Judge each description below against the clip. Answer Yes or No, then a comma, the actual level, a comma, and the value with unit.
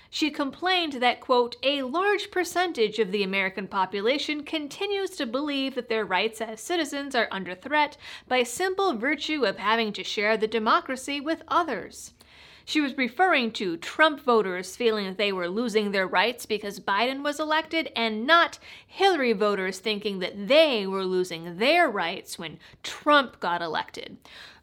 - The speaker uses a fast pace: No, average, 160 wpm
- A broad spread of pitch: Yes, wide, 6.7 semitones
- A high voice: Yes, very high, 250 Hz